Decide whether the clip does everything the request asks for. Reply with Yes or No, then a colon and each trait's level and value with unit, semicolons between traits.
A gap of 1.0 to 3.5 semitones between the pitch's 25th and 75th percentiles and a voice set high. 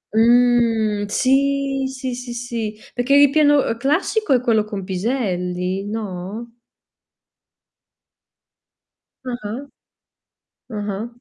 No: average, 4.2 semitones; high, 235 Hz